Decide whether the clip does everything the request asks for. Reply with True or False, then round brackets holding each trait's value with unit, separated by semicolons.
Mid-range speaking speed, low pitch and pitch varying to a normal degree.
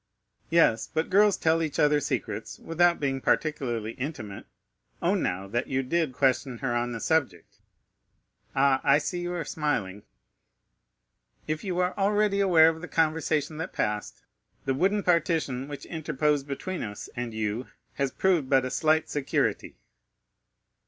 False (150 wpm; 150 Hz; 4.3 semitones)